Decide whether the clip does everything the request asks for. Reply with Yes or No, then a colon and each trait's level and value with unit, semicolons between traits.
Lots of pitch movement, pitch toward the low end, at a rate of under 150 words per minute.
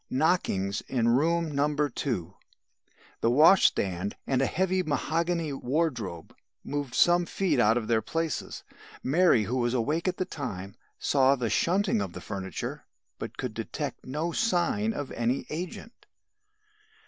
No: wide, 6.4 semitones; medium, 145 Hz; average, 140 wpm